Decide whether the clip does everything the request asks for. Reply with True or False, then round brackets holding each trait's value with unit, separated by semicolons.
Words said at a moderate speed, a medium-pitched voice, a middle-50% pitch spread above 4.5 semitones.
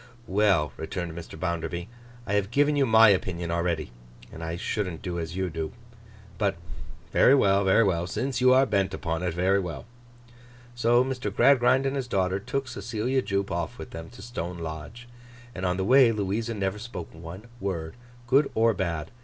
False (180 wpm; 95 Hz; 5.3 semitones)